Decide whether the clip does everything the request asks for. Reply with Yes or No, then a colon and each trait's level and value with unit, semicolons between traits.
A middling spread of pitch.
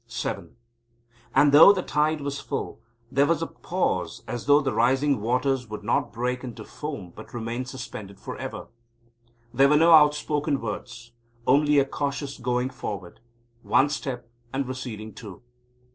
Yes: average, 3.6 semitones